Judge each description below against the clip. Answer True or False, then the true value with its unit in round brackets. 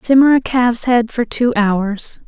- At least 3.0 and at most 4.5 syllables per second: True (4.3 syllables/s)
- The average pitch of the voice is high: True (235 Hz)